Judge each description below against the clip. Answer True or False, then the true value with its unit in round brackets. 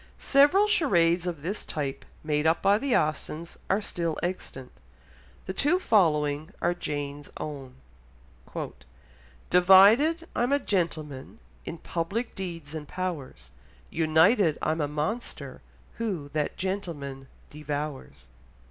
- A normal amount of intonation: True (5.0 semitones)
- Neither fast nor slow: False (115 wpm)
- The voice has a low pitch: False (165 Hz)